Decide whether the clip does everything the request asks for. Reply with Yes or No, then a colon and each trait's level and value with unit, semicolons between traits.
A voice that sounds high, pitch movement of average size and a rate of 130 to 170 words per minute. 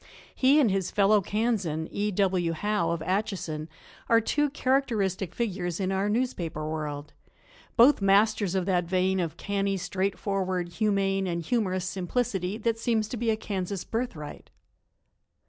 Yes: high, 195 Hz; average, 3.4 semitones; average, 145 wpm